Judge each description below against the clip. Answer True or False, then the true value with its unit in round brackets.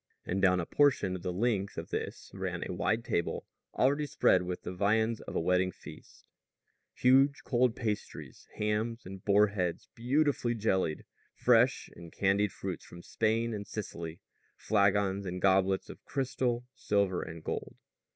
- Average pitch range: True (4.1 semitones)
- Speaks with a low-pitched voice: True (100 Hz)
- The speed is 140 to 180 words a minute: True (150 wpm)